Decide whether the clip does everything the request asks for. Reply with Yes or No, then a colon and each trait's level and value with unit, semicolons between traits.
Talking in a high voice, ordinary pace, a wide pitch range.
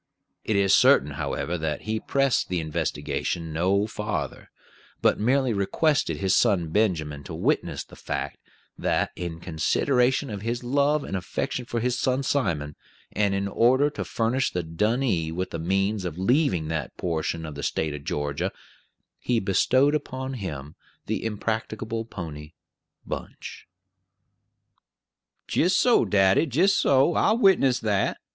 No: low, 100 Hz; average, 145 wpm; wide, 7.5 semitones